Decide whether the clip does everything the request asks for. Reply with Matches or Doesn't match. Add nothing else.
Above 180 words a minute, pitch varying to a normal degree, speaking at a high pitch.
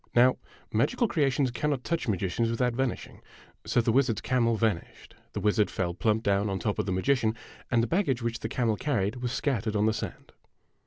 Doesn't match